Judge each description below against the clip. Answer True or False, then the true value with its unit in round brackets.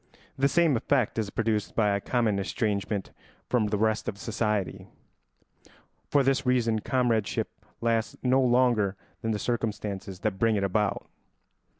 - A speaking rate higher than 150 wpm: False (140 wpm)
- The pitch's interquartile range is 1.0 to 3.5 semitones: True (3.0 semitones)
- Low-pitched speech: True (110 Hz)